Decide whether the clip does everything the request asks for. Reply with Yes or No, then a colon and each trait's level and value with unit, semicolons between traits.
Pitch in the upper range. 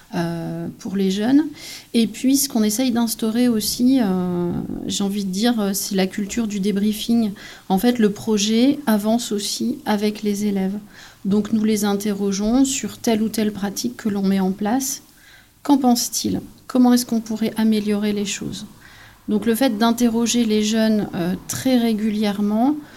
Yes: high, 215 Hz